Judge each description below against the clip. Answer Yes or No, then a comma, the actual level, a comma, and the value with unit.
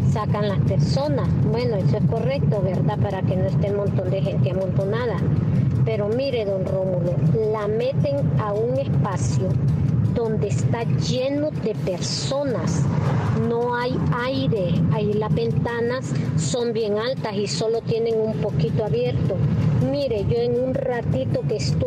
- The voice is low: No, medium, 150 Hz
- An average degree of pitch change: Yes, average, 3.9 semitones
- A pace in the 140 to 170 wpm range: Yes, average, 145 wpm